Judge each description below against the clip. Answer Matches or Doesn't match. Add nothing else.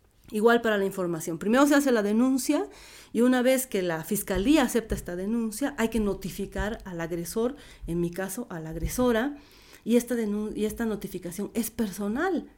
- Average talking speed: Matches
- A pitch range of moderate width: Matches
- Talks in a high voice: Matches